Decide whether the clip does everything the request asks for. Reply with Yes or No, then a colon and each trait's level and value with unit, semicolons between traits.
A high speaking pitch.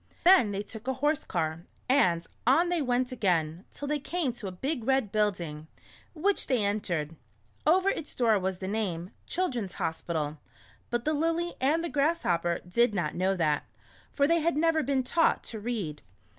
Yes: high, 235 Hz